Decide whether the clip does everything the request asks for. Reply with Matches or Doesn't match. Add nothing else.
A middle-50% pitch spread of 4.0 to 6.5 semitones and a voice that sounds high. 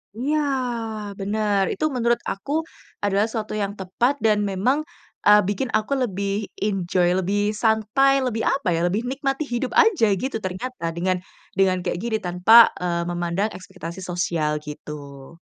Matches